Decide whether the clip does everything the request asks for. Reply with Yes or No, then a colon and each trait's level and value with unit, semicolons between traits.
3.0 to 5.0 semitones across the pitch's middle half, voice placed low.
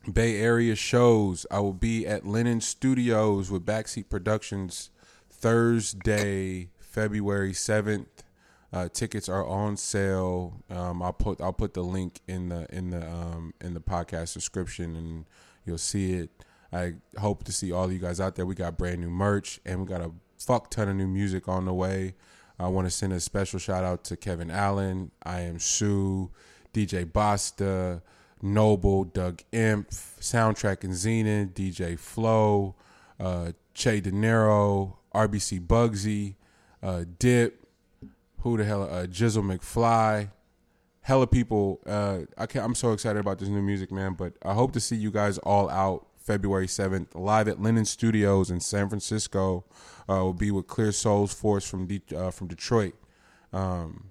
No: narrow, 2.6 semitones; low, 100 Hz